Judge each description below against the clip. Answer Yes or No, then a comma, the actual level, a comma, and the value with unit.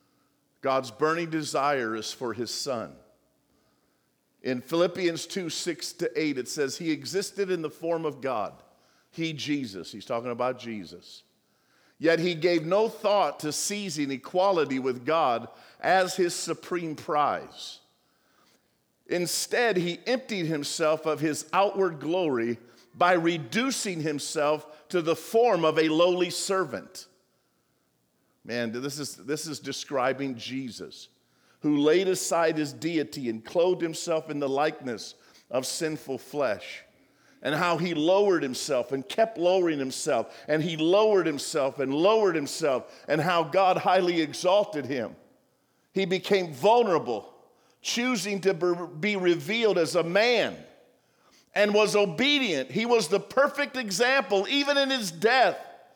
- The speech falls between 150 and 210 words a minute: No, slow, 135 wpm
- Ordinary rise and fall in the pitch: Yes, average, 4.6 semitones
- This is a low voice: No, medium, 165 Hz